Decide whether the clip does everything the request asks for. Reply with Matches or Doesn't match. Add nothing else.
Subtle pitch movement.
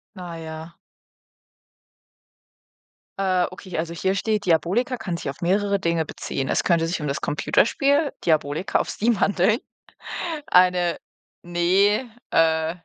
Doesn't match